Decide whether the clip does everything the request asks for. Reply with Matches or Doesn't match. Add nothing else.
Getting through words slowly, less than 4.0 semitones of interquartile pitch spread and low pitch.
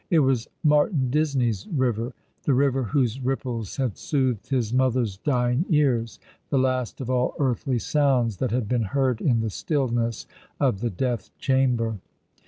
Doesn't match